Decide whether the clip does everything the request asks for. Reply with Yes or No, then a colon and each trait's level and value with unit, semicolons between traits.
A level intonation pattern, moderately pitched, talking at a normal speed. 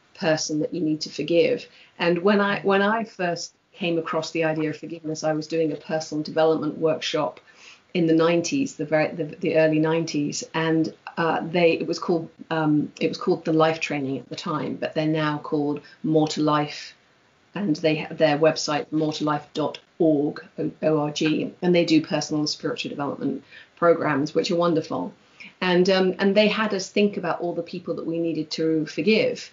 Yes: narrow, 1.9 semitones; medium, 160 Hz; average, 190 wpm